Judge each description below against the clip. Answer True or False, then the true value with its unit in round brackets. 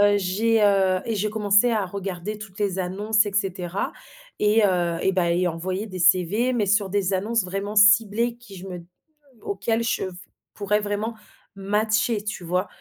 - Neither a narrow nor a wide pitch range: False (2.3 semitones)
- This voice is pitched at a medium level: False (200 Hz)